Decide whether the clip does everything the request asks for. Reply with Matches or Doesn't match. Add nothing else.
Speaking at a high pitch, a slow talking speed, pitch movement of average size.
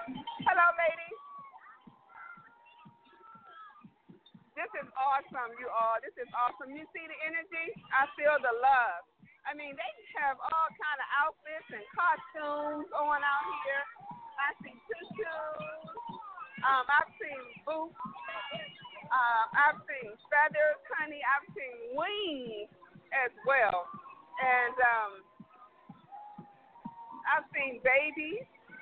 Doesn't match